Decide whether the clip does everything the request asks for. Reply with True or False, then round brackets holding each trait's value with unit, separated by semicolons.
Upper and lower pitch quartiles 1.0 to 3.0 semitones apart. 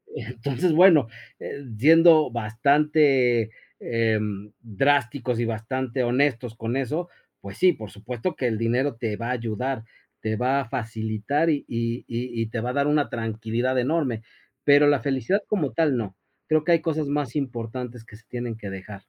False (4.1 semitones)